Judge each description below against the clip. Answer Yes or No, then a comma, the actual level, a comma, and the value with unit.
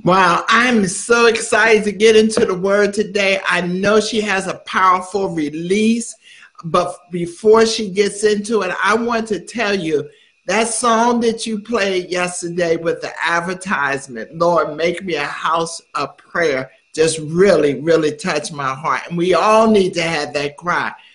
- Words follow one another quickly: No, average, 165 wpm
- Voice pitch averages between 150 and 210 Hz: Yes, high, 190 Hz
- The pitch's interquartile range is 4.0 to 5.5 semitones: Yes, average, 4.6 semitones